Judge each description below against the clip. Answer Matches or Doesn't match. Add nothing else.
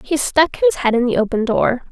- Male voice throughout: Doesn't match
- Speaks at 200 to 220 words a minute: Doesn't match